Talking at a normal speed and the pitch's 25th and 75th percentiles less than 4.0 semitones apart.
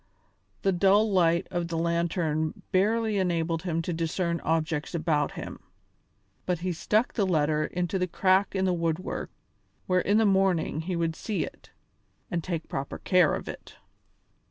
Yes: average, 160 wpm; narrow, 2.6 semitones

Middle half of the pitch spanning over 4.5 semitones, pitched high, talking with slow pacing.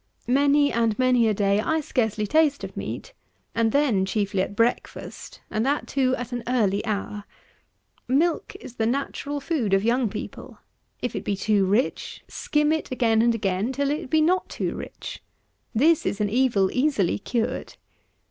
No: average, 5.1 semitones; high, 240 Hz; average, 170 wpm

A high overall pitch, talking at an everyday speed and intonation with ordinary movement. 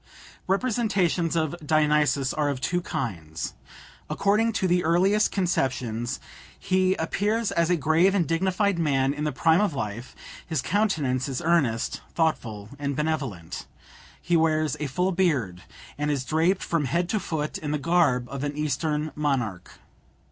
No: medium, 155 Hz; average, 150 wpm; average, 4.7 semitones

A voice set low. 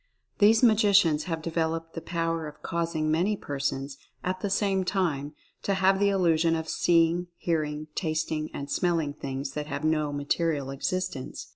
No: medium, 165 Hz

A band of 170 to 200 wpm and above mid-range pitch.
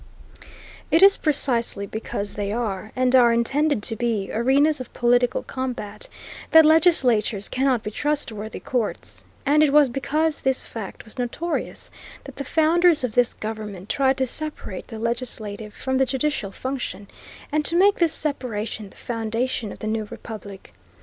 No: average, 155 wpm; high, 245 Hz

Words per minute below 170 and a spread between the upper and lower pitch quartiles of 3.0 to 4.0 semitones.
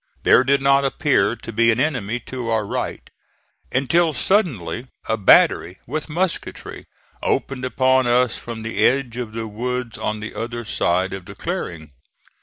Yes: average, 160 wpm; average, 3.5 semitones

